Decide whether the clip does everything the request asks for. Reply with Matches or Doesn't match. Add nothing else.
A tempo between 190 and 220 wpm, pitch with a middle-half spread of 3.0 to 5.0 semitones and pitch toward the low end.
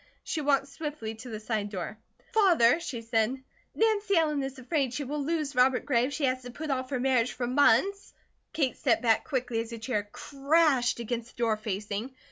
Doesn't match